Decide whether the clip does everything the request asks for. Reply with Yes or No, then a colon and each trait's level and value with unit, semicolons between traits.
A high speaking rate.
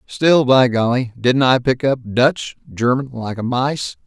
No: average, 150 wpm